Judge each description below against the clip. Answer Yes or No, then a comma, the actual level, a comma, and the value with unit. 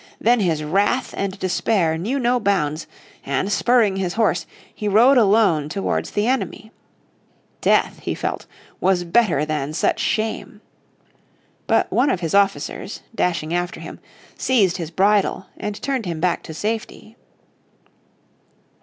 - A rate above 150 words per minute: No, slow, 135 wpm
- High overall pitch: Yes, high, 195 Hz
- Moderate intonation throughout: Yes, average, 4.5 semitones